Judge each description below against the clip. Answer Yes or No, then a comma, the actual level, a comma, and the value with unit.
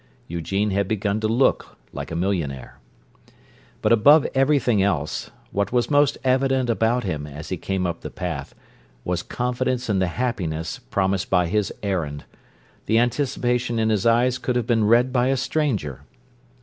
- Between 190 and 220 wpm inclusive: No, average, 160 wpm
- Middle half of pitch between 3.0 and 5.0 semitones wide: No, wide, 5.4 semitones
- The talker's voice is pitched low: Yes, low, 110 Hz